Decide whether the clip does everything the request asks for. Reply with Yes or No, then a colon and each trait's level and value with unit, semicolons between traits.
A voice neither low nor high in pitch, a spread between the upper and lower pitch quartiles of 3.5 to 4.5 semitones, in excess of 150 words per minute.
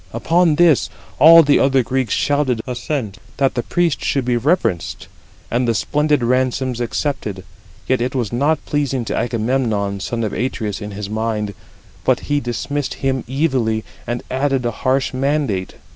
No: low, 130 Hz; average, 4.0 semitones; average, 160 wpm